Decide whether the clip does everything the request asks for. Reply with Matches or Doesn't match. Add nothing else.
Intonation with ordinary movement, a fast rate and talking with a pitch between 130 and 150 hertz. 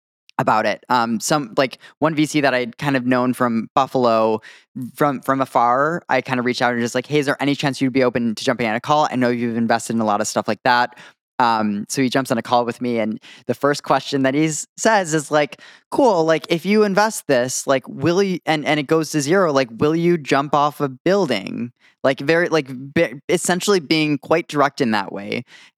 Matches